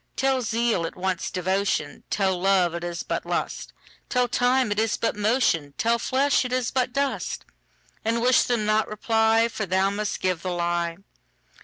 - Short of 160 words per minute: Yes, average, 150 wpm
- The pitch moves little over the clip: No, average, 4.7 semitones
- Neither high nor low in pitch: No, high, 215 Hz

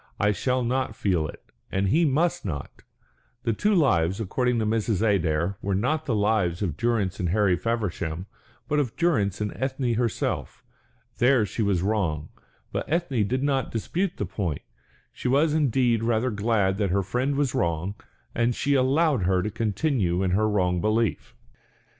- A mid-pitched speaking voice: No, low, 110 Hz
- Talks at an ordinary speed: Yes, average, 170 wpm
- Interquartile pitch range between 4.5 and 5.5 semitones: Yes, average, 5.2 semitones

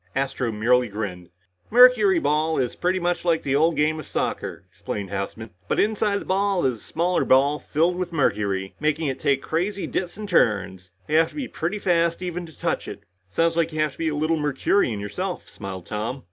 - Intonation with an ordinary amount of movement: No, wide, 6.8 semitones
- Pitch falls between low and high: Yes, medium, 155 Hz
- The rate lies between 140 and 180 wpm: No, average, 200 wpm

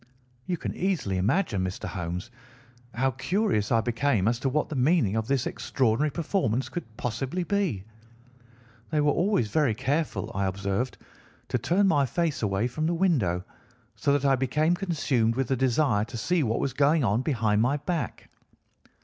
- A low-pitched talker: Yes, low, 130 Hz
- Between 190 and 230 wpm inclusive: No, average, 170 wpm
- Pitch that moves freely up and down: Yes, wide, 5.9 semitones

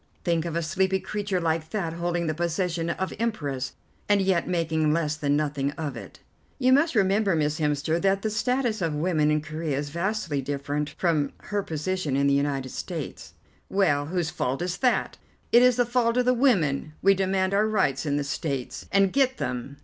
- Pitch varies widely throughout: No, average, 4.9 semitones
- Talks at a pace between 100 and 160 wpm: No, average, 195 wpm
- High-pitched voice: No, medium, 170 Hz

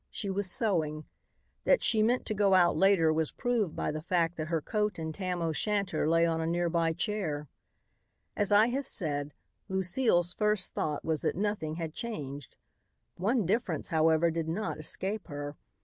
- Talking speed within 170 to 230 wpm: Yes, average, 180 wpm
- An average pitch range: Yes, average, 4.6 semitones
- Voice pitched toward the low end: No, medium, 175 Hz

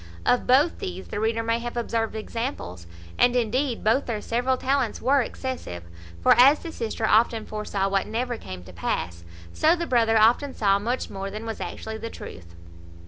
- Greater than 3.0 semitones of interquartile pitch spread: Yes, average, 3.4 semitones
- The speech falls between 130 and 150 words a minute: No, average, 185 wpm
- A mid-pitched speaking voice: No, high, 225 Hz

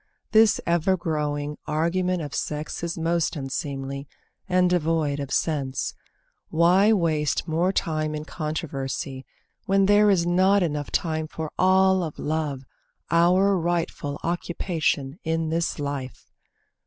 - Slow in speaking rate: Yes, slow, 125 wpm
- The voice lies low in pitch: No, medium, 165 Hz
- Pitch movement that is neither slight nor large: Yes, average, 3.2 semitones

